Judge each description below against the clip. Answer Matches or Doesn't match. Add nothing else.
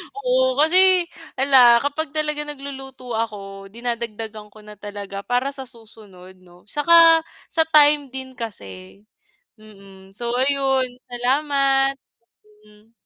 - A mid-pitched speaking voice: Doesn't match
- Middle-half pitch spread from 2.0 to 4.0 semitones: Doesn't match